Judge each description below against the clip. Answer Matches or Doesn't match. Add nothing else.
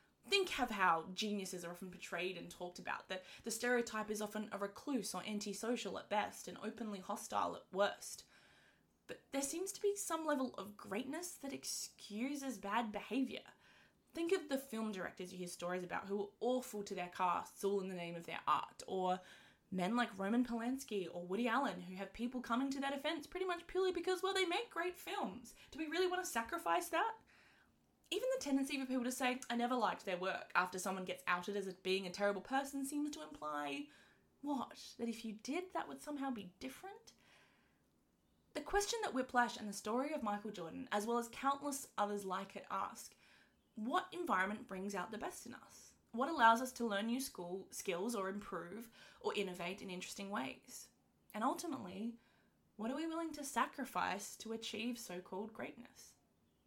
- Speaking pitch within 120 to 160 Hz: Doesn't match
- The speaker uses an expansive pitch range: Matches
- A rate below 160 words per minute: Doesn't match